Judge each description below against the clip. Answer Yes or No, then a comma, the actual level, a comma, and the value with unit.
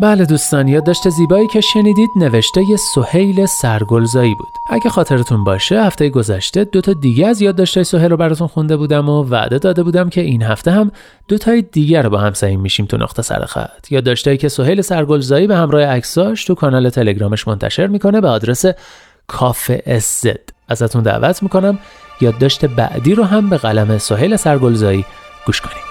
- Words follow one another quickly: Yes, fast, 180 wpm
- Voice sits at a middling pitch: Yes, medium, 155 Hz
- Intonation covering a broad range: Yes, wide, 7.8 semitones